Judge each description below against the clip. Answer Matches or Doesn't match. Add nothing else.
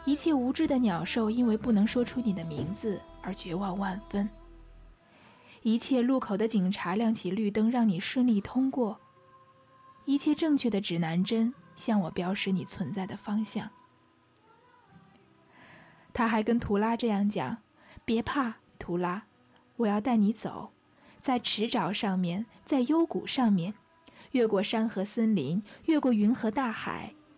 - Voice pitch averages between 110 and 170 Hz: Doesn't match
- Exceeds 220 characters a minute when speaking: Doesn't match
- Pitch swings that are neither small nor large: Matches